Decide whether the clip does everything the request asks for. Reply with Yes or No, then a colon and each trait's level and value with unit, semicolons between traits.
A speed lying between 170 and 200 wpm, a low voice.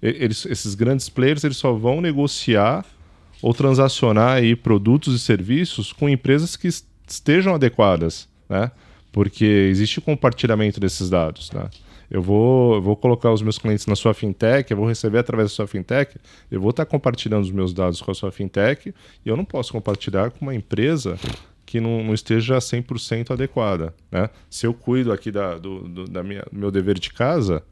Yes: average, 180 wpm; low, 110 Hz